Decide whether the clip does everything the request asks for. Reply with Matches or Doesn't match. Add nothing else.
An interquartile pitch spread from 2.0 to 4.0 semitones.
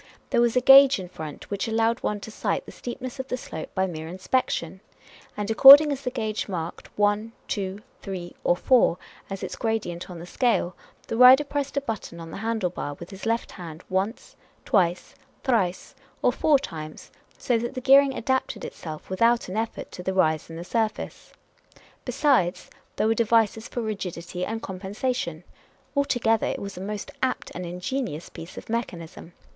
Doesn't match